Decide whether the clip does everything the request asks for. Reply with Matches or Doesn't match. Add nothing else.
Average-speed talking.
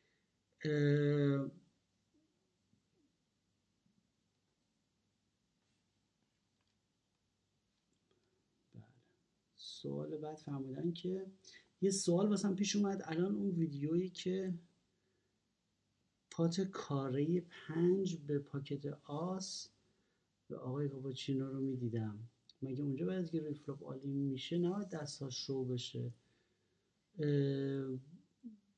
Doesn't match